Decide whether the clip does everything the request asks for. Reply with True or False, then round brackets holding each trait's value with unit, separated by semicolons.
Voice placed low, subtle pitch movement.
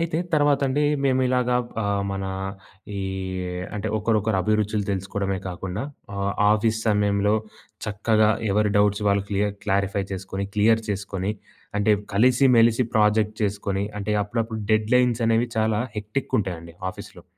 True (105 Hz; 2.3 semitones)